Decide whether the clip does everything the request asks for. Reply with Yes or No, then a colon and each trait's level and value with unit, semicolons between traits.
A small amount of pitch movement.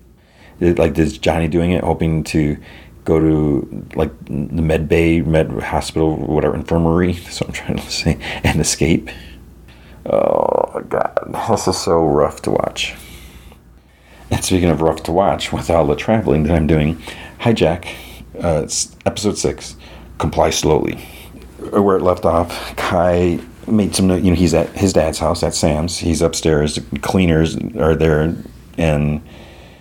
Yes: narrow, 1.9 semitones